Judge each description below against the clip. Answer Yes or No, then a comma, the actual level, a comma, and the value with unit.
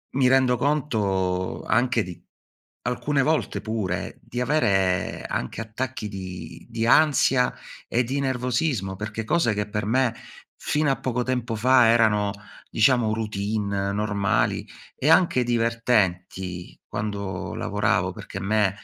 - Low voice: Yes, low, 110 Hz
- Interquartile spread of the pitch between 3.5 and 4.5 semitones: Yes, average, 4.2 semitones